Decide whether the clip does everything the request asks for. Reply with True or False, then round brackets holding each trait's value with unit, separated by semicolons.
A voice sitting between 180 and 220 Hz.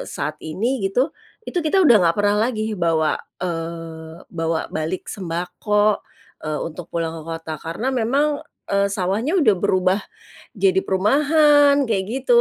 True (190 Hz)